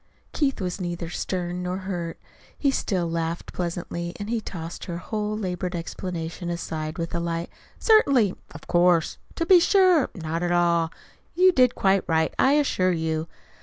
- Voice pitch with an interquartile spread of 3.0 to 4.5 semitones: Yes, average, 4.0 semitones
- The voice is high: No, medium, 175 Hz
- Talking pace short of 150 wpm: No, average, 165 wpm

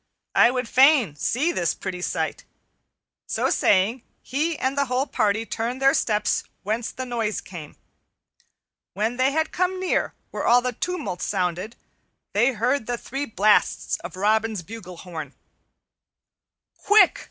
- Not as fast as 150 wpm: Yes, average, 140 wpm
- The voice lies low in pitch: No, high, 230 Hz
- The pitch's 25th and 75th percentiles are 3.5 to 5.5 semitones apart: Yes, average, 4.9 semitones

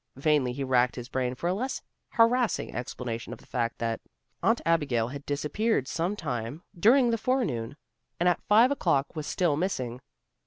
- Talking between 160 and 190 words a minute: Yes, average, 170 wpm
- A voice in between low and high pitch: Yes, medium, 145 Hz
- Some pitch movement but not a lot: No, wide, 8.6 semitones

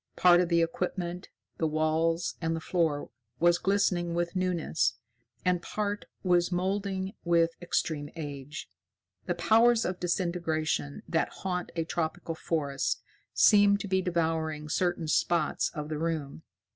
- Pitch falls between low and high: Yes, medium, 170 Hz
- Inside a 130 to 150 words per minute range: Yes, slow, 135 wpm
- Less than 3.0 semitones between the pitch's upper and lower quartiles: Yes, narrow, 2.4 semitones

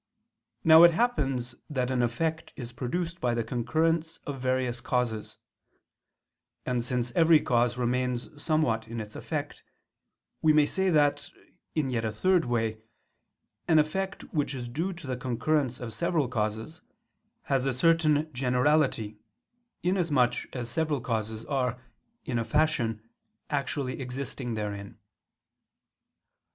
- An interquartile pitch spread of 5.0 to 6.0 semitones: No, average, 4.6 semitones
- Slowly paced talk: Yes, slow, 130 wpm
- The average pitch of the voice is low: Yes, low, 130 Hz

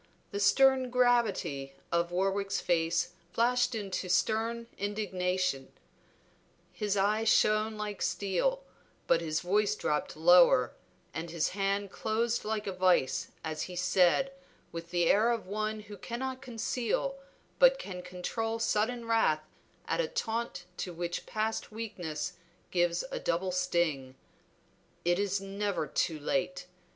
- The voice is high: Yes, high, 195 Hz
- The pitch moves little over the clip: No, average, 4.2 semitones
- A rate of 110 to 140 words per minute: Yes, slow, 135 wpm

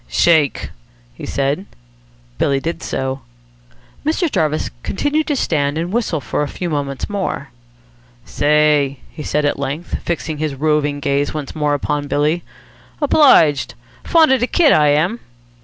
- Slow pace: No, average, 145 wpm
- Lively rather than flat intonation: No, average, 3.6 semitones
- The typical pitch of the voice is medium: Yes, medium, 150 Hz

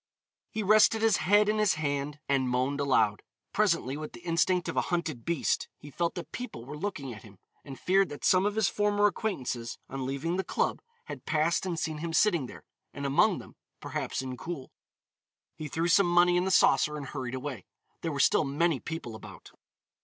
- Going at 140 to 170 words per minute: No, average, 200 wpm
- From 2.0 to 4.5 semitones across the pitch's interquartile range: No, average, 5.3 semitones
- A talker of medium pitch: Yes, medium, 160 Hz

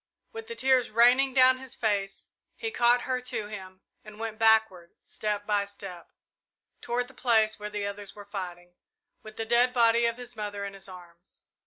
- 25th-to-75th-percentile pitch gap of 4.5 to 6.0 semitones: No, average, 3.5 semitones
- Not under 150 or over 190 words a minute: Yes, average, 185 wpm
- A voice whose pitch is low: No, high, 220 Hz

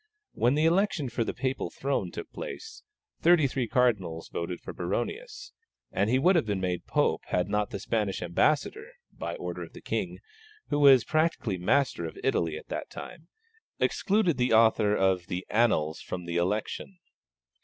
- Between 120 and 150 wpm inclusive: No, average, 170 wpm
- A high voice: No, low, 115 Hz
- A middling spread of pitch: No, wide, 8.8 semitones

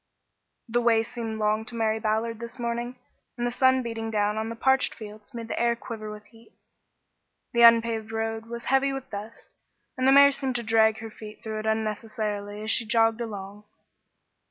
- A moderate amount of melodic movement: No, narrow, 1.6 semitones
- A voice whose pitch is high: Yes, high, 225 Hz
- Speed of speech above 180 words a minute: Yes, average, 190 wpm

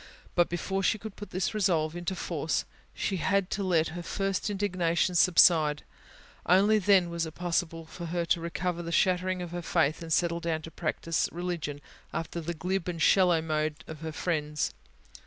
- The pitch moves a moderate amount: No, narrow, 2.2 semitones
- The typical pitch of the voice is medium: Yes, medium, 170 Hz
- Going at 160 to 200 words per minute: Yes, average, 180 wpm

